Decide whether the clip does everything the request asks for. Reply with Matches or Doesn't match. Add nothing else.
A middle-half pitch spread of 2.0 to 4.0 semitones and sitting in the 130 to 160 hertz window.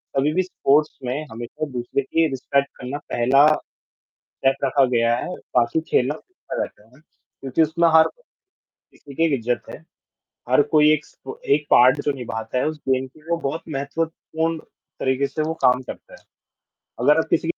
Matches